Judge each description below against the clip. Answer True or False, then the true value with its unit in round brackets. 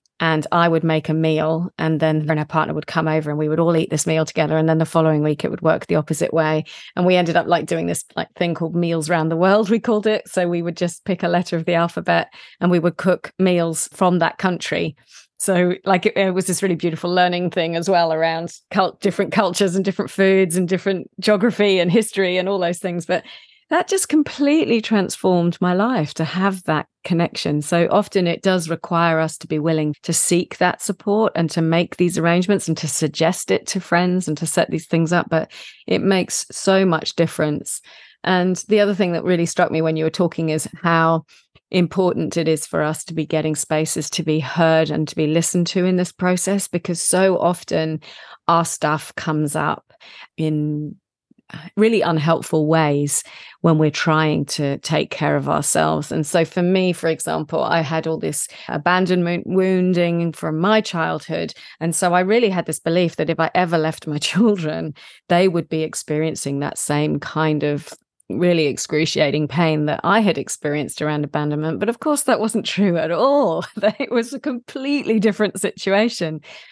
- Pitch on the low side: False (170 Hz)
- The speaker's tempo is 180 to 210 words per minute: True (200 wpm)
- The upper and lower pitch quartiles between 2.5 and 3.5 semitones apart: True (2.9 semitones)